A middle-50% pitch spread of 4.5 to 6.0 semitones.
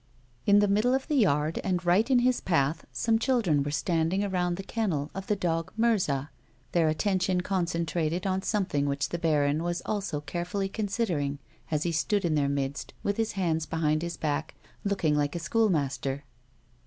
Yes: average, 4.9 semitones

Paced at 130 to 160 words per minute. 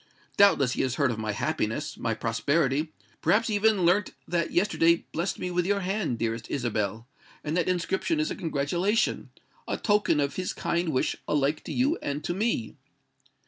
No: average, 170 wpm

